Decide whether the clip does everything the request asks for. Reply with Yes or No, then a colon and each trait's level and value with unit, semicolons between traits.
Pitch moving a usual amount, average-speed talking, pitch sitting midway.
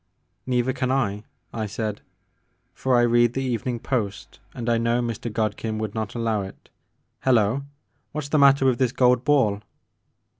No: average, 3.0 semitones; average, 185 wpm; low, 120 Hz